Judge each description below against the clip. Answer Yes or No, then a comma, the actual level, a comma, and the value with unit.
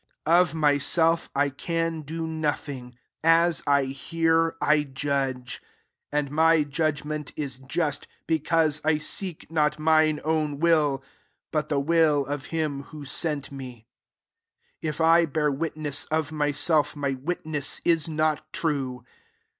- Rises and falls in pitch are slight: Yes, narrow, 2.3 semitones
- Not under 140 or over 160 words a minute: Yes, average, 145 wpm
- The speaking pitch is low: No, medium, 150 Hz